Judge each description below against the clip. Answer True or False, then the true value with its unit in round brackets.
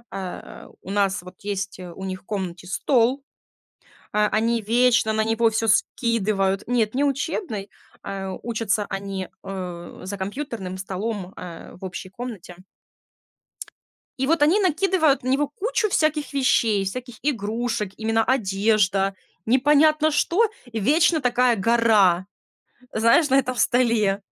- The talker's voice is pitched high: True (225 Hz)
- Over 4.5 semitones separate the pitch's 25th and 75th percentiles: True (5.0 semitones)